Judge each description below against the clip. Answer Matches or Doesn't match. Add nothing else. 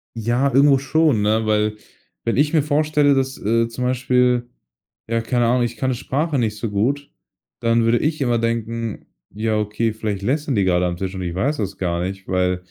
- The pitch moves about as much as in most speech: Matches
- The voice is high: Doesn't match